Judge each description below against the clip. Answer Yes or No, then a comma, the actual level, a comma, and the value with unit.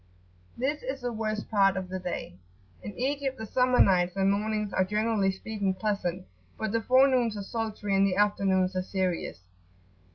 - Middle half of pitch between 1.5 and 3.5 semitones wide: Yes, average, 3.2 semitones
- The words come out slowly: No, average, 170 wpm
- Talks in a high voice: Yes, high, 205 Hz